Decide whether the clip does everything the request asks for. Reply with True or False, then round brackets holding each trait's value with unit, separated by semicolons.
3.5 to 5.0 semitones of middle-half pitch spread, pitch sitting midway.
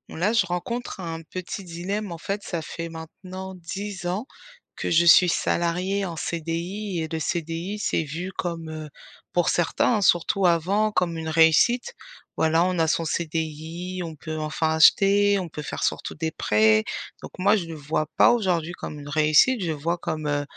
False (2.9 semitones; 170 Hz)